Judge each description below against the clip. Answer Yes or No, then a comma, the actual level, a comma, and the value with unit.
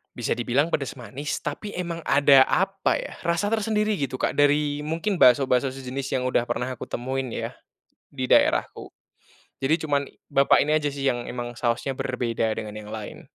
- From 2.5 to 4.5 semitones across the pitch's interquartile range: Yes, average, 3.3 semitones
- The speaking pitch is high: No, low, 135 Hz